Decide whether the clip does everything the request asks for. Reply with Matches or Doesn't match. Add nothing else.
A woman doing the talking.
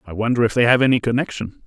Doesn't match